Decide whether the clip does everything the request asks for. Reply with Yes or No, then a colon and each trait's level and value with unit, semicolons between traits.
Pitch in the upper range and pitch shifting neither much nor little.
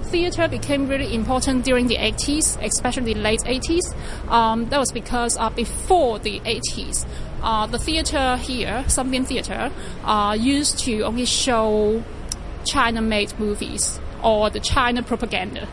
Yes: high, 240 Hz; average, 3.3 semitones